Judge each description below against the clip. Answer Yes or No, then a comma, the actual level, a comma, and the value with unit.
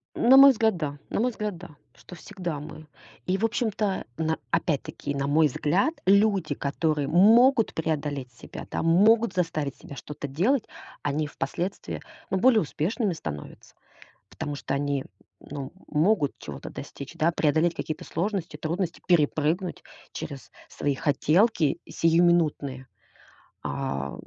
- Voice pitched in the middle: Yes, medium, 160 Hz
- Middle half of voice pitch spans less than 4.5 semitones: No, average, 5.2 semitones